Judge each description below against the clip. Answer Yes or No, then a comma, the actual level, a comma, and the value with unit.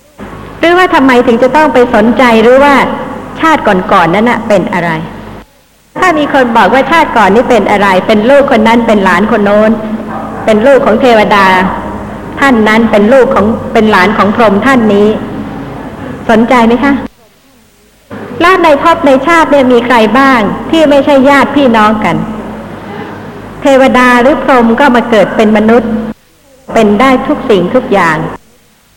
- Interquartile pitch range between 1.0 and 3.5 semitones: No, average, 3.9 semitones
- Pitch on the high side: Yes, high, 240 Hz